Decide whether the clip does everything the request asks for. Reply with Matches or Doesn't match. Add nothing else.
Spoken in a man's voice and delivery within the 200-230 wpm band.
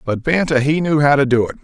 Doesn't match